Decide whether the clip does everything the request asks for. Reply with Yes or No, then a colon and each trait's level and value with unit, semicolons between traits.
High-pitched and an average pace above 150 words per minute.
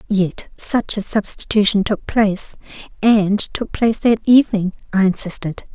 No: high, 205 Hz; slow, 135 wpm